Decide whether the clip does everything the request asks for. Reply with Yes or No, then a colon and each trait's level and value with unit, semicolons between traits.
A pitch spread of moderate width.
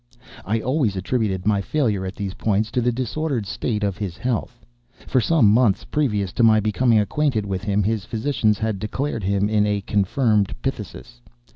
Yes: average, 3.5 semitones